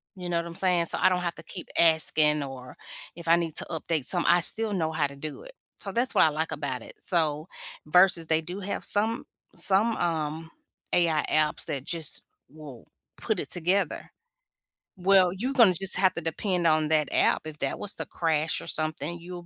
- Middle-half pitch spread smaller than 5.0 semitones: Yes, average, 2.9 semitones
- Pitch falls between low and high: Yes, medium, 170 Hz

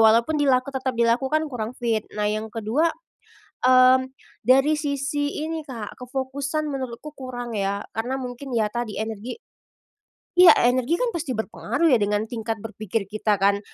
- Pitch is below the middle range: No, high, 245 Hz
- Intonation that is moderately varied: Yes, average, 3.8 semitones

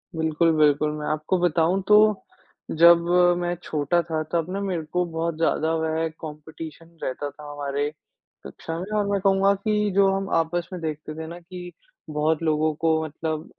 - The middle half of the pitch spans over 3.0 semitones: No, narrow, 2.5 semitones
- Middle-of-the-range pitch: Yes, medium, 165 Hz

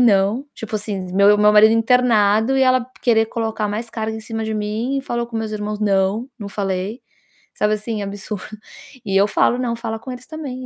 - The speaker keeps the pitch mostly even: Yes, narrow, 2.3 semitones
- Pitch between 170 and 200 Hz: No, high, 220 Hz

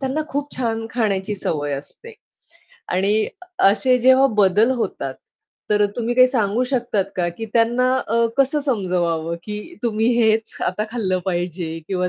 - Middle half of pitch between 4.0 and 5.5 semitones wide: Yes, average, 5.0 semitones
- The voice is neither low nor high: No, high, 220 Hz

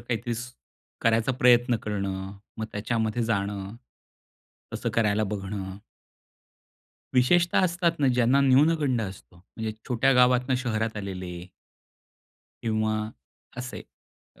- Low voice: Yes, low, 115 Hz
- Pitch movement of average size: Yes, average, 3.5 semitones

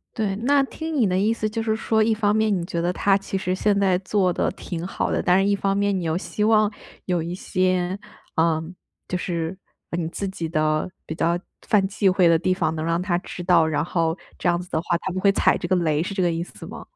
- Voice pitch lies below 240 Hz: Yes, medium, 185 Hz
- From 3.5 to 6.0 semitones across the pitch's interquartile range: No, average, 3.1 semitones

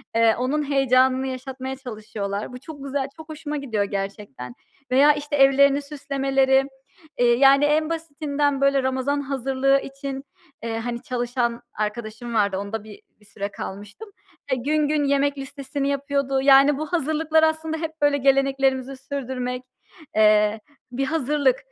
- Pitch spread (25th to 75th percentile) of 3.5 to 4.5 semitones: No, average, 2.9 semitones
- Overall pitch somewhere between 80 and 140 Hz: No, very high, 270 Hz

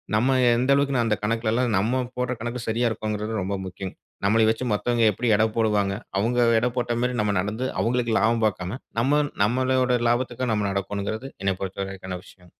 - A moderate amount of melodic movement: Yes, average, 3.3 semitones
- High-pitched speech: No, low, 115 Hz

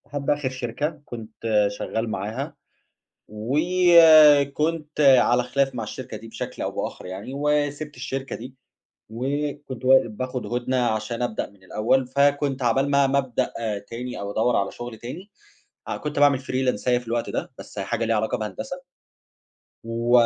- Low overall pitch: Yes, low, 130 Hz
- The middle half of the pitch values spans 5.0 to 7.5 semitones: No, average, 3.7 semitones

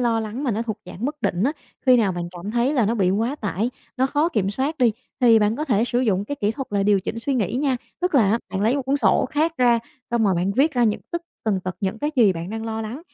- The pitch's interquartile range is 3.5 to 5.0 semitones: Yes, average, 4.5 semitones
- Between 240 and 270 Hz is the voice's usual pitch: No, high, 230 Hz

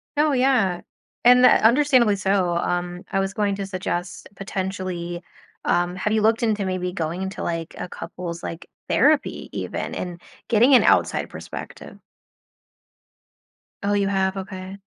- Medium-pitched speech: No, high, 195 Hz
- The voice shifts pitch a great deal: No, average, 3.5 semitones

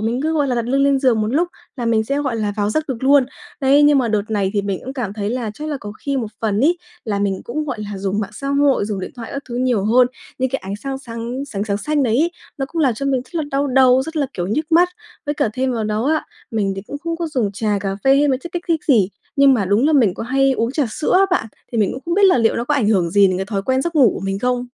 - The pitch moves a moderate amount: Yes, average, 4.8 semitones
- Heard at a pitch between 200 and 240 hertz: No, very high, 250 Hz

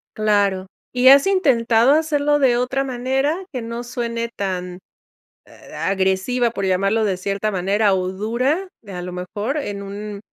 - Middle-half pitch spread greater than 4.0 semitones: Yes, average, 4.7 semitones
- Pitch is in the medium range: No, high, 225 Hz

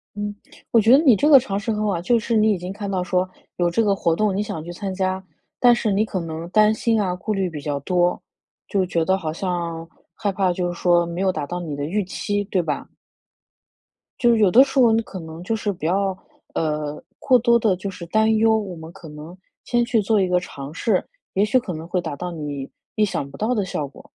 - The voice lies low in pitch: No, high, 190 Hz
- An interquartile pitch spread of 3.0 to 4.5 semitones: Yes, average, 4.0 semitones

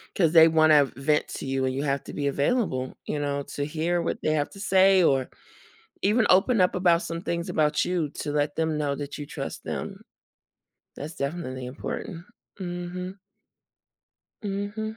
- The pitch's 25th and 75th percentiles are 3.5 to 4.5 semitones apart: Yes, average, 4.2 semitones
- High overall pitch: No, medium, 160 Hz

